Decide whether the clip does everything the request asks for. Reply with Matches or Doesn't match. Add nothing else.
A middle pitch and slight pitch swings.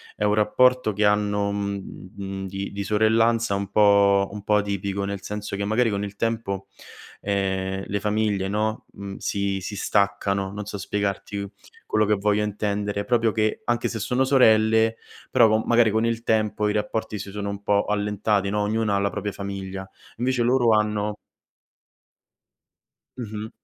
Doesn't match